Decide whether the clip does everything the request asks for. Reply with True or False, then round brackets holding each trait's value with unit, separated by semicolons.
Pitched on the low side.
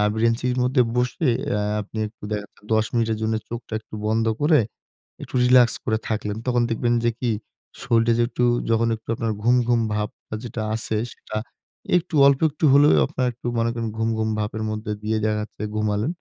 True (115 Hz)